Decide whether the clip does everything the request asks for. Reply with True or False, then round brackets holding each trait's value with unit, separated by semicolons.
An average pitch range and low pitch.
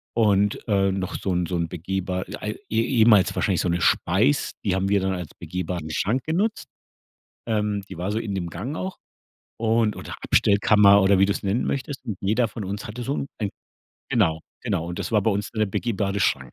True (3.0 semitones; 100 Hz)